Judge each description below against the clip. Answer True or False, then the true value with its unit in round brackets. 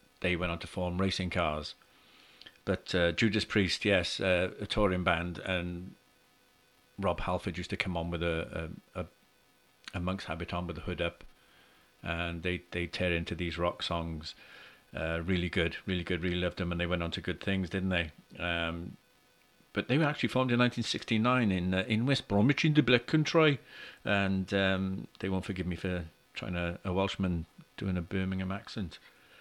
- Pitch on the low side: True (90 Hz)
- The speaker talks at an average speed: True (190 wpm)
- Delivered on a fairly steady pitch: True (2.3 semitones)